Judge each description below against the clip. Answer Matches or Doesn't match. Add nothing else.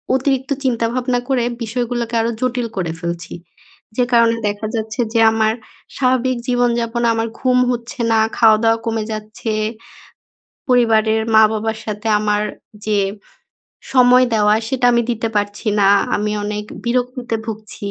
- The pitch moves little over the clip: Matches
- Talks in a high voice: Matches